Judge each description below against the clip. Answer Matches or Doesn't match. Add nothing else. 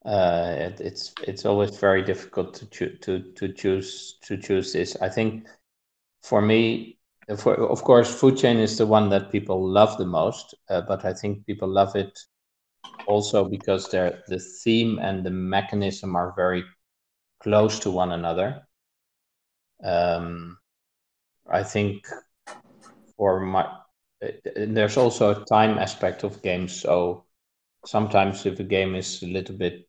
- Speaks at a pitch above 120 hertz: Doesn't match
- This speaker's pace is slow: Doesn't match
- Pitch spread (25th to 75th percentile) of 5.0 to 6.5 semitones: Doesn't match